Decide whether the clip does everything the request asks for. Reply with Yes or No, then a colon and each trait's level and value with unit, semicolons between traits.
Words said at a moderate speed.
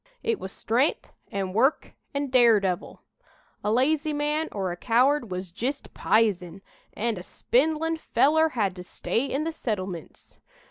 Yes: average, 145 wpm